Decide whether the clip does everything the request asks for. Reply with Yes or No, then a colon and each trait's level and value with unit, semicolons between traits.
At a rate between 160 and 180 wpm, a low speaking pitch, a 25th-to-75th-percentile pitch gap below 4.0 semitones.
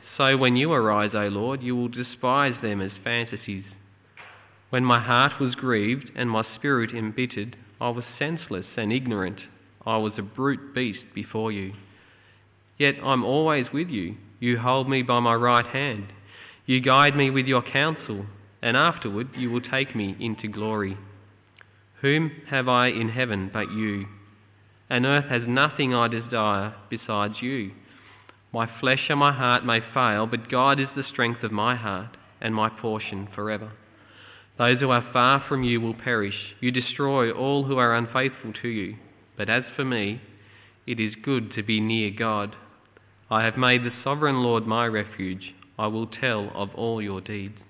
Yes: average, 170 wpm; low, 115 Hz; average, 3.4 semitones